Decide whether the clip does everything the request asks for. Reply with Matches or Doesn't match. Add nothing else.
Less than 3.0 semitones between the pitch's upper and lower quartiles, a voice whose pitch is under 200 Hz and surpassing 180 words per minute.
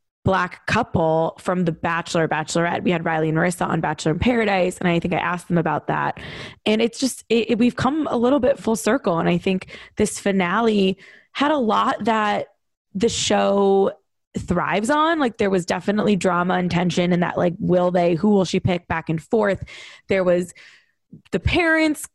Doesn't match